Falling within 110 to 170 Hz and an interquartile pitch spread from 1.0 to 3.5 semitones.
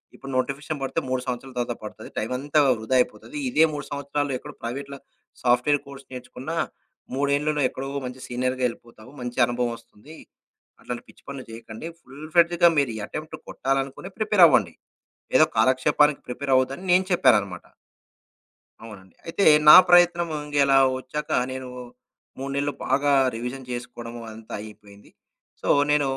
Yes: low, 135 Hz; average, 3.2 semitones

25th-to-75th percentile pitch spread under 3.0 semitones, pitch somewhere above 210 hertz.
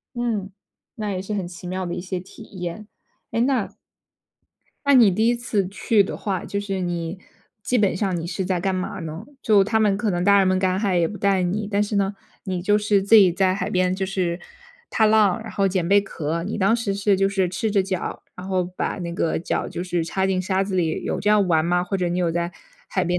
No: narrow, 2.4 semitones; high, 190 Hz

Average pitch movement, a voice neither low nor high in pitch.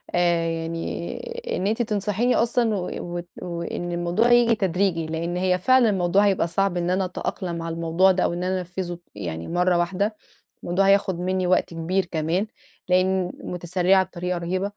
No: narrow, 2.1 semitones; medium, 180 Hz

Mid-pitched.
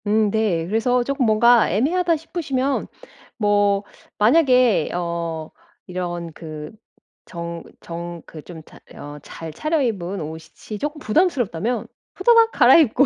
No: high, 210 Hz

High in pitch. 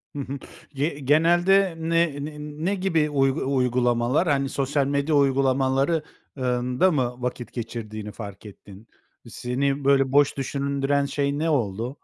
No: medium, 140 Hz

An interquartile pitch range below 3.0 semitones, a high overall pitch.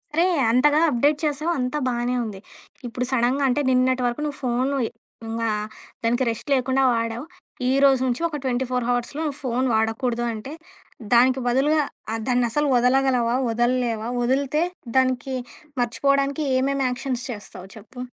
Yes: narrow, 2.4 semitones; very high, 255 Hz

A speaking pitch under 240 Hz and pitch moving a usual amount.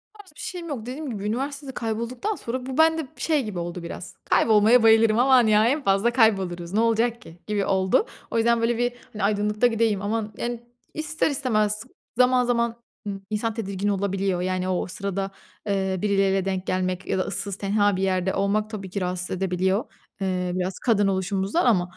Yes: high, 210 Hz; average, 3.7 semitones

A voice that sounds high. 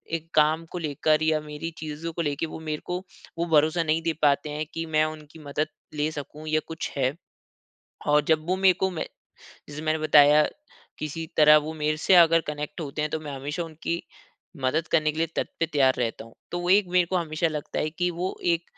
No: medium, 155 Hz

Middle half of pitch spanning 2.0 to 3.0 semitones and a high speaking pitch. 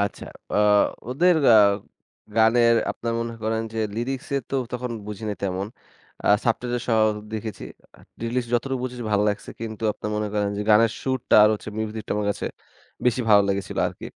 No: narrow, 2.5 semitones; low, 115 Hz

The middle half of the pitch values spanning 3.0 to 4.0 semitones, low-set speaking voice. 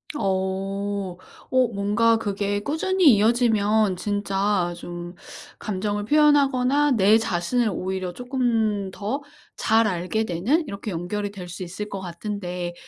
No: average, 3.4 semitones; high, 205 Hz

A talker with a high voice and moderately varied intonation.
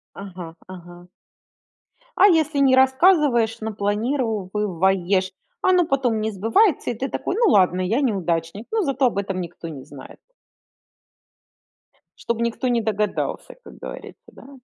No: high, 220 Hz; wide, 6.0 semitones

